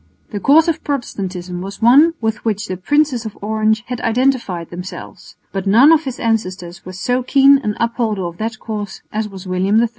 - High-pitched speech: Yes, high, 220 Hz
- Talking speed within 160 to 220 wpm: Yes, average, 190 wpm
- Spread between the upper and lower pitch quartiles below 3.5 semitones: No, average, 4.7 semitones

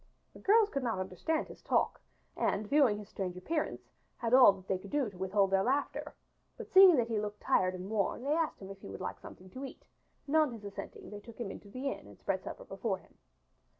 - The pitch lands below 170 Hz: No, high, 220 Hz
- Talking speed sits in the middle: No, fast, 235 wpm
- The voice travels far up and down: Yes, wide, 6.4 semitones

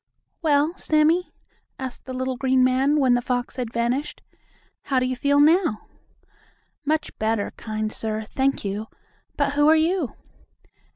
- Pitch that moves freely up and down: No, average, 3.5 semitones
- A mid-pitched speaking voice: No, very high, 260 Hz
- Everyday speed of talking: Yes, average, 150 wpm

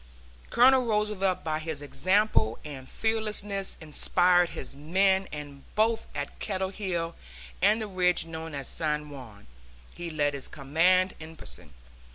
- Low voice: No, medium, 175 Hz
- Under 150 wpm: Yes, average, 140 wpm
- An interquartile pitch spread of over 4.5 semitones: Yes, average, 4.9 semitones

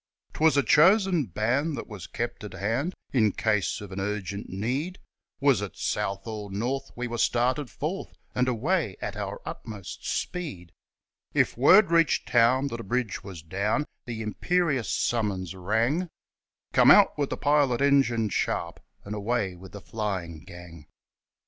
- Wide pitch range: Yes, wide, 5.9 semitones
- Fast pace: No, average, 155 wpm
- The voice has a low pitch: Yes, low, 115 Hz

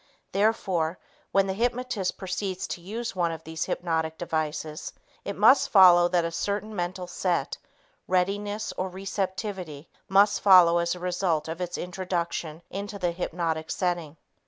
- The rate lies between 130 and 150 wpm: Yes, average, 145 wpm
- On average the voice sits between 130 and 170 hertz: No, medium, 180 Hz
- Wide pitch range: No, narrow, 2.6 semitones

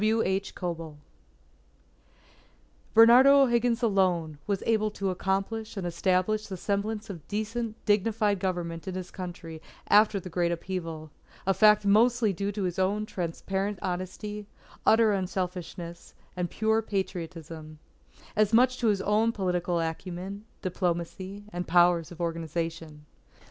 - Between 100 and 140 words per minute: Yes, slow, 135 wpm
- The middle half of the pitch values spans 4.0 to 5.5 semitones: No, average, 3.6 semitones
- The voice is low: No, high, 190 Hz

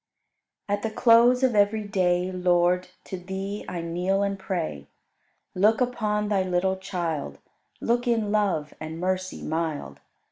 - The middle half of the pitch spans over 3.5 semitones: No, average, 3.0 semitones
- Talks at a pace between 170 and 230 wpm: No, average, 145 wpm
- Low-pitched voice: No, high, 190 Hz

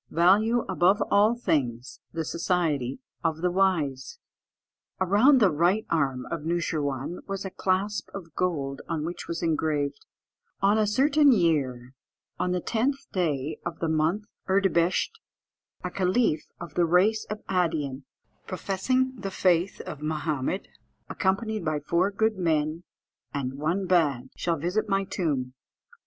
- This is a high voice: No, medium, 175 Hz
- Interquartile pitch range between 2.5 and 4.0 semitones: No, average, 4.5 semitones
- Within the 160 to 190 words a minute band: No, average, 140 wpm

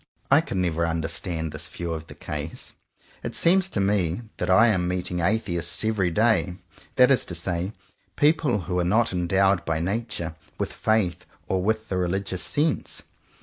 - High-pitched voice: No, very low, 90 Hz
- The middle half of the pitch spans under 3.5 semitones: No, average, 4.2 semitones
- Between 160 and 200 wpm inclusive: Yes, average, 170 wpm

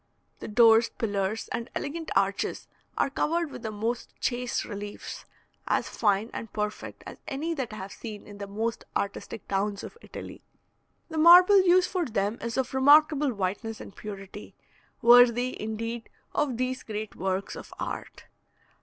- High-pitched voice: Yes, high, 230 Hz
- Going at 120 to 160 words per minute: Yes, average, 155 wpm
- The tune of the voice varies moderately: Yes, average, 4.6 semitones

